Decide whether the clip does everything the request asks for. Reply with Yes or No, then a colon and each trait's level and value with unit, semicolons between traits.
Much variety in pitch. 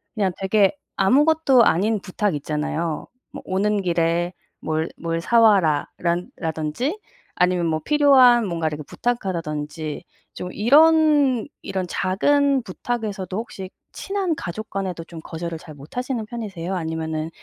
Yes: wide, 6.5 semitones